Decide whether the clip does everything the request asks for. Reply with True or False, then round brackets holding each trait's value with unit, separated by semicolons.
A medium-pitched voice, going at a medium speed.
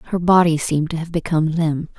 False (165 Hz; 210 wpm)